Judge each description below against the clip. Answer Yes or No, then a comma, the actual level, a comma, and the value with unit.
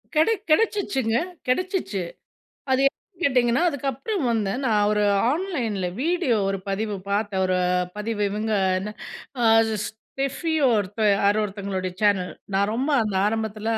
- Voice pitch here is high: Yes, high, 220 Hz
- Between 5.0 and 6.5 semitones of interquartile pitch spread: Yes, wide, 5.4 semitones